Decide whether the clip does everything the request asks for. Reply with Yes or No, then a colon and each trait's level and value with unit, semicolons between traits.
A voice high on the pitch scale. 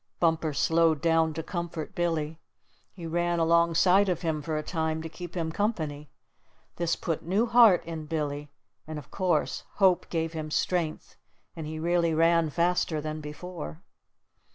No: medium, 165 Hz